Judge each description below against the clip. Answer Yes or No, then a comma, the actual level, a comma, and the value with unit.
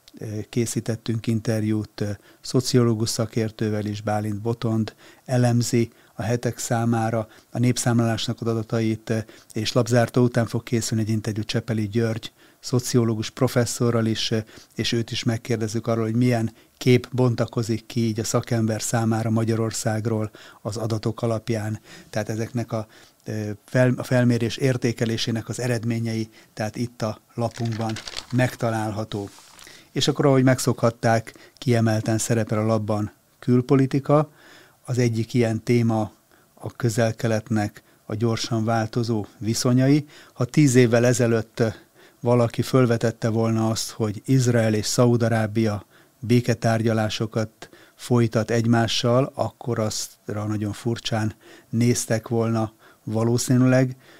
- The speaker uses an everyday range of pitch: No, narrow, 1.5 semitones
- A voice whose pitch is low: Yes, low, 115 Hz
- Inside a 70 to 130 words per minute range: Yes, average, 110 wpm